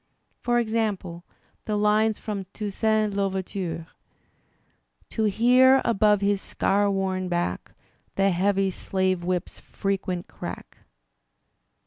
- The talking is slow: Yes, slow, 105 wpm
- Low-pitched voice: No, high, 200 Hz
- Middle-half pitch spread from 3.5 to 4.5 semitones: No, narrow, 2.4 semitones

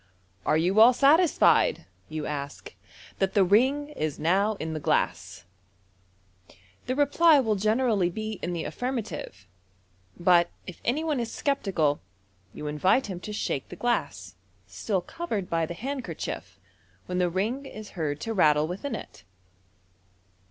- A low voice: No, high, 200 Hz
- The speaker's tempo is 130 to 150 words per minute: Yes, average, 145 wpm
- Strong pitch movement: Yes, wide, 7.2 semitones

